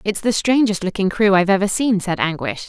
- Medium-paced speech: No, fast, 225 wpm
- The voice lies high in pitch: Yes, high, 200 Hz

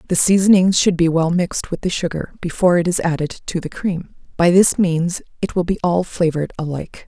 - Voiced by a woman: Yes, female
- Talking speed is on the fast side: Yes, fast, 210 wpm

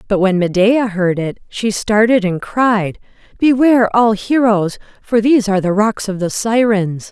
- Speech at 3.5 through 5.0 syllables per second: Yes, 4.5 syllables/s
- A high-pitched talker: Yes, high, 210 Hz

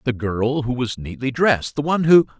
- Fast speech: Yes, fast, 225 wpm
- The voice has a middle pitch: No, low, 130 Hz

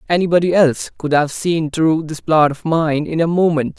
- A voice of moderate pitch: Yes, medium, 160 Hz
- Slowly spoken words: No, fast, 205 wpm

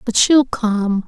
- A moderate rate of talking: Yes, average, 165 wpm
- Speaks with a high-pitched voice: Yes, high, 230 Hz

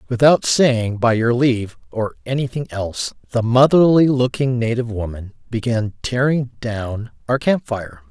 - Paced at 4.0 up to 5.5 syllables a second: Yes, 4.5 syllables/s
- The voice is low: Yes, low, 120 Hz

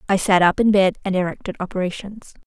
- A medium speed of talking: Yes, average, 195 wpm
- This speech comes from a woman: Yes, female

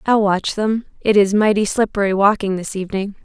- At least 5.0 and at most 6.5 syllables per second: Yes, 5.5 syllables/s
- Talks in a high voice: Yes, high, 205 Hz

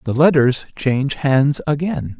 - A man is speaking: Yes, male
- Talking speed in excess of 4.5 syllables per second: No, 4.1 syllables/s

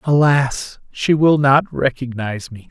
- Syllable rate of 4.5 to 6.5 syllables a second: No, 4.0 syllables/s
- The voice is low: Yes, low, 130 Hz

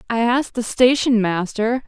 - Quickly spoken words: No, average, 160 wpm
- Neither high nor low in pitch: No, high, 230 Hz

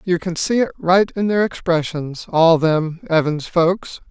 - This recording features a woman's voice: No, male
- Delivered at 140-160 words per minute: No, average, 175 wpm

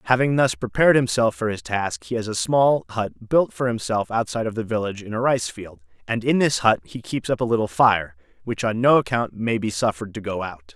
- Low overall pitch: Yes, low, 110 Hz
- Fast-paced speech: Yes, fast, 240 wpm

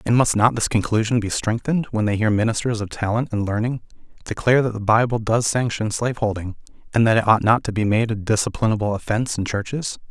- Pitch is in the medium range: No, low, 110 Hz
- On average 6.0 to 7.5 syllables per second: Yes, 6.3 syllables/s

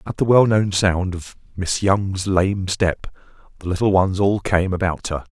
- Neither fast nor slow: Yes, average, 180 wpm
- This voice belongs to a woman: No, male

